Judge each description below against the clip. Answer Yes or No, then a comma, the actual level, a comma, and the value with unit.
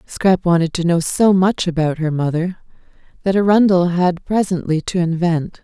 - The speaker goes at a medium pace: Yes, average, 160 wpm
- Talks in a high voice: No, medium, 175 Hz